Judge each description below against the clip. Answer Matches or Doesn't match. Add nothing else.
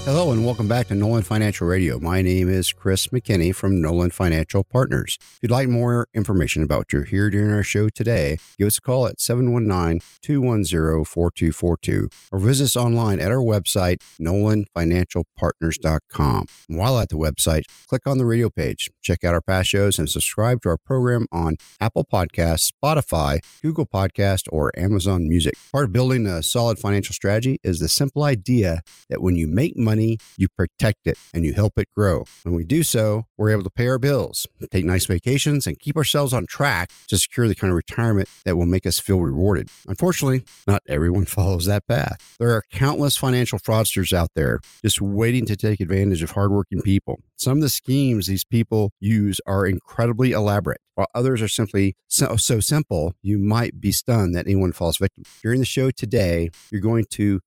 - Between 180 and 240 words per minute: Matches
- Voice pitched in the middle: Doesn't match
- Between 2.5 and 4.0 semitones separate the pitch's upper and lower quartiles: Doesn't match